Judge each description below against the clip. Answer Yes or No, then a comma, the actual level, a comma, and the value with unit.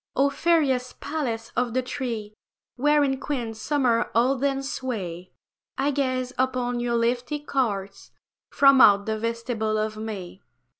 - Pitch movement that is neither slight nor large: Yes, average, 3.5 semitones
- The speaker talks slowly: Yes, slow, 130 wpm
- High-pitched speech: Yes, high, 245 Hz